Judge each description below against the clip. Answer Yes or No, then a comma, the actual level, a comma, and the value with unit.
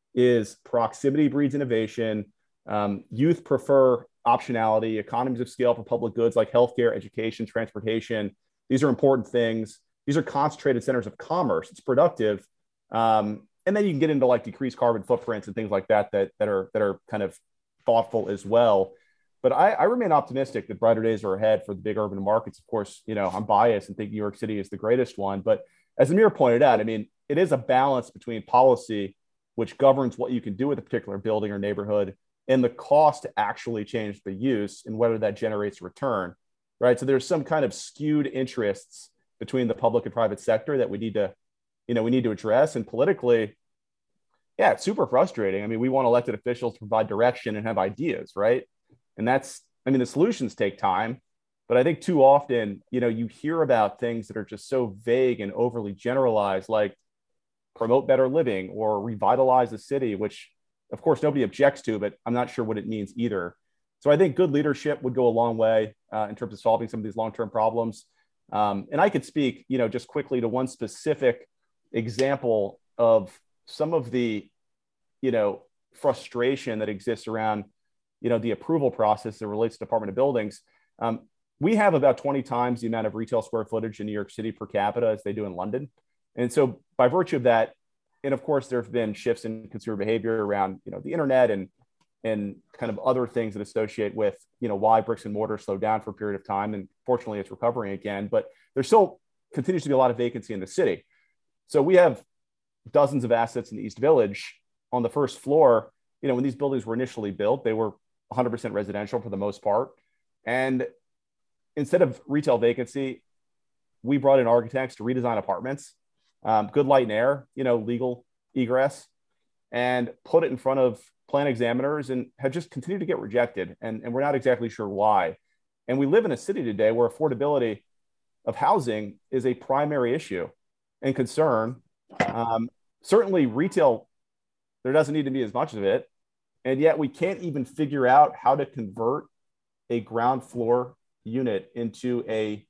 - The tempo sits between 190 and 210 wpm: Yes, average, 200 wpm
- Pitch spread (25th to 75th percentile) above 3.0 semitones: Yes, average, 3.5 semitones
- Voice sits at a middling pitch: No, low, 120 Hz